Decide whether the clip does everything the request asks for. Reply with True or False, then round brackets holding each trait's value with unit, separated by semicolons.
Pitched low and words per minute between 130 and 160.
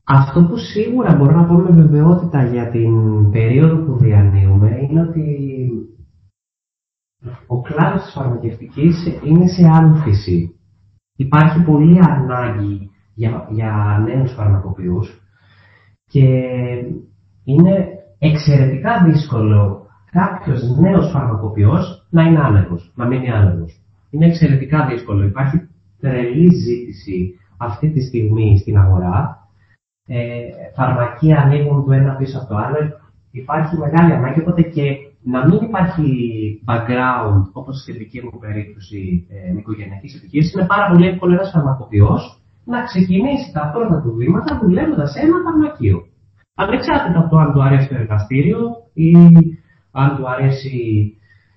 False (130 Hz; 120 wpm)